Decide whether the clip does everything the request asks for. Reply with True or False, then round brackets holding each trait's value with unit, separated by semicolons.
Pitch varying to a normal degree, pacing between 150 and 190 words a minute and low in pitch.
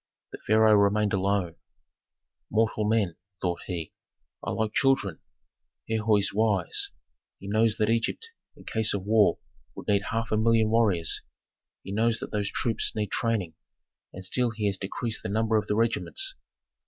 False (2.1 semitones; 165 wpm; 110 Hz)